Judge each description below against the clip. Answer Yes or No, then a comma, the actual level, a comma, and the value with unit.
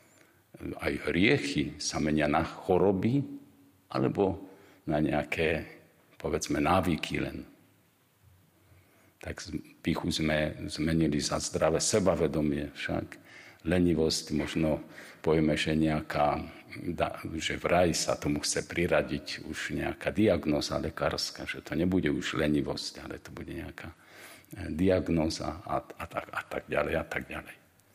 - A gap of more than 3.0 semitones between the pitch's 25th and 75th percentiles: Yes, average, 3.8 semitones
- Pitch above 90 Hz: No, very low, 80 Hz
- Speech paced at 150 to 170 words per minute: No, average, 115 wpm